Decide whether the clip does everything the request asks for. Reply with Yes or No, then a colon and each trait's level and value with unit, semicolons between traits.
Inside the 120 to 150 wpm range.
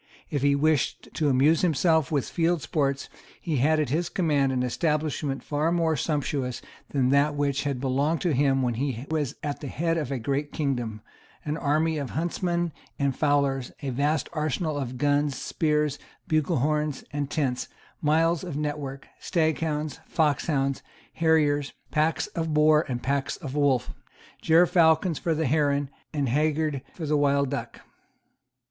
No: average, 160 wpm